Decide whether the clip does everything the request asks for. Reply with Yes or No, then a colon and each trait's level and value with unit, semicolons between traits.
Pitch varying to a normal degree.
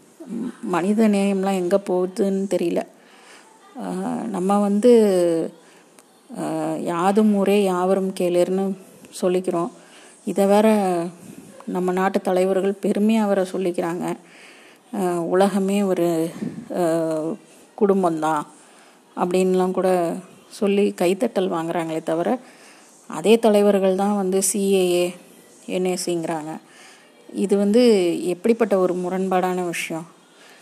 No: narrow, 2.3 semitones